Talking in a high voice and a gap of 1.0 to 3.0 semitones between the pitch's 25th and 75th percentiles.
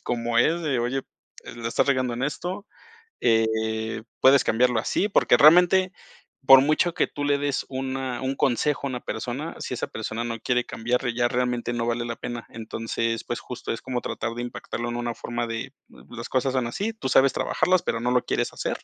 No: low, 125 Hz; narrow, 2.6 semitones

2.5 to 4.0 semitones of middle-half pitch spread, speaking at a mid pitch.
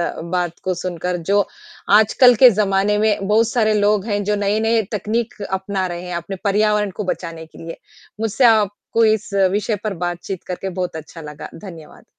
No: average, 3.0 semitones; high, 200 Hz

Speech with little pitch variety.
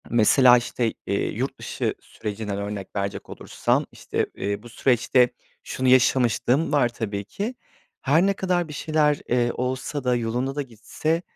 No: average, 4.3 semitones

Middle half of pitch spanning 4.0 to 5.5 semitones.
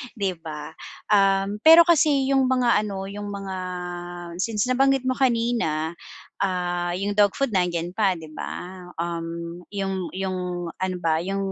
Yes: average, 4.6 semitones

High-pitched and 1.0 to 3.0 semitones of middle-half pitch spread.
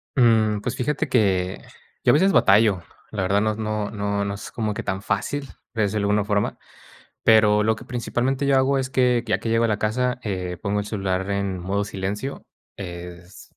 No: low, 105 Hz; average, 2.7 semitones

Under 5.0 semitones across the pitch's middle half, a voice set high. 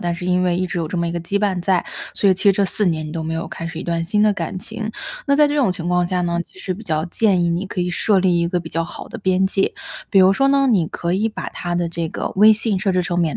No: average, 2.7 semitones; medium, 180 Hz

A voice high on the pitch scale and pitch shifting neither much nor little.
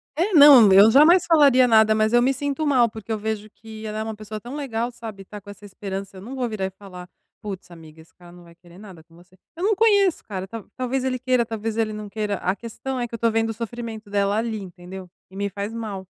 Yes: high, 220 Hz; average, 3.6 semitones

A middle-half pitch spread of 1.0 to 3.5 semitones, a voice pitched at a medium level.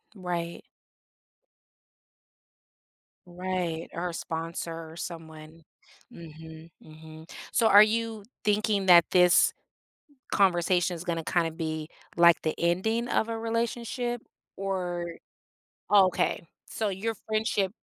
No: average, 4.0 semitones; medium, 175 Hz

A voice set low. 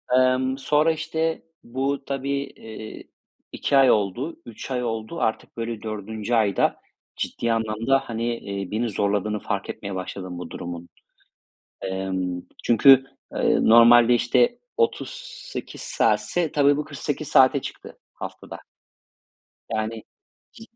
Yes: low, 120 Hz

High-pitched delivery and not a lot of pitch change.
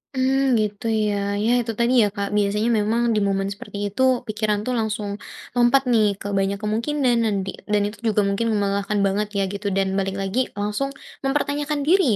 No: high, 215 Hz; average, 3.5 semitones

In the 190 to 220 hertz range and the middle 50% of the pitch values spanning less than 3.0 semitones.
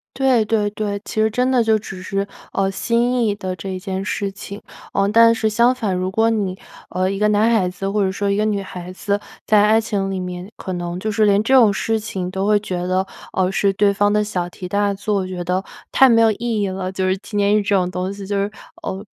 Yes: high, 200 Hz; narrow, 2.4 semitones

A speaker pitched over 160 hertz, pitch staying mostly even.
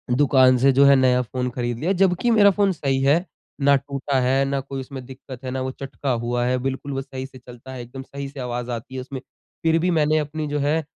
No: low, 135 Hz; narrow, 2.1 semitones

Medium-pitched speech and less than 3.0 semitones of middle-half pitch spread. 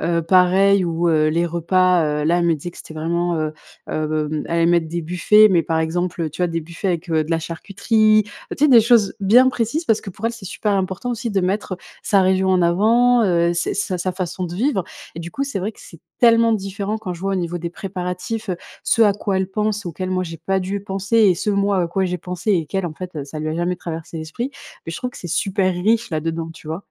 No: medium, 180 Hz; average, 3.3 semitones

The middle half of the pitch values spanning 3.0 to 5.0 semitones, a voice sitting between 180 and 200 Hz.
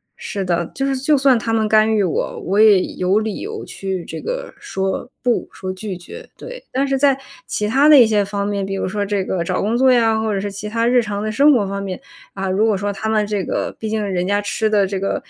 No: average, 3.3 semitones; high, 210 Hz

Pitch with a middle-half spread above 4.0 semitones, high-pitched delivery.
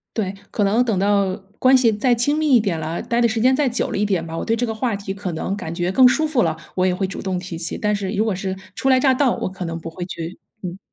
Yes: average, 4.7 semitones; high, 200 Hz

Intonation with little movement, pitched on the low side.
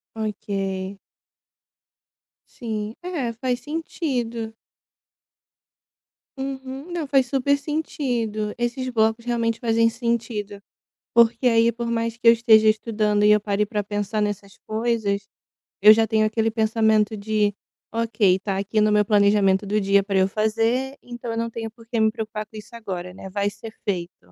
No: narrow, 2.2 semitones; high, 220 Hz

